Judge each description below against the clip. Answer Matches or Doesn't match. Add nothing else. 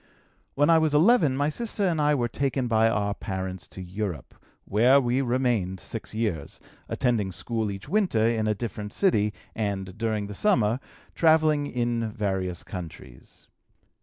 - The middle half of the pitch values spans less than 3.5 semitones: Doesn't match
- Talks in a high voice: Doesn't match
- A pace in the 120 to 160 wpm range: Matches